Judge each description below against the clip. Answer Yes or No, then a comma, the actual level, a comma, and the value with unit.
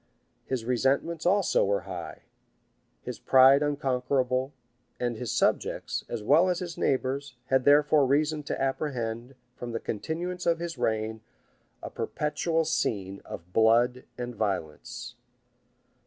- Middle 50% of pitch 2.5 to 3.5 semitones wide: No, average, 4.5 semitones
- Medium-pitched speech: No, low, 130 Hz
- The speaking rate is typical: No, slow, 125 wpm